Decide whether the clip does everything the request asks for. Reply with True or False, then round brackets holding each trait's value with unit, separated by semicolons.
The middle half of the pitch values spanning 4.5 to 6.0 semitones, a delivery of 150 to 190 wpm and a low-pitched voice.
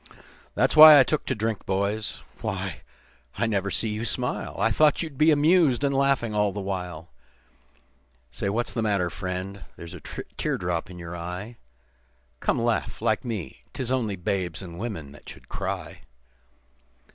True (5.5 semitones; 165 wpm; 105 Hz)